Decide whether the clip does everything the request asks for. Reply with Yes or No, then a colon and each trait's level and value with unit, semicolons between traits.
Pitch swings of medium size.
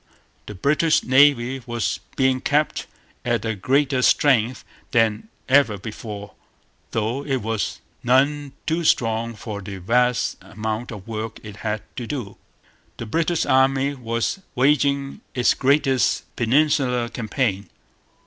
Yes: average, 3.8 semitones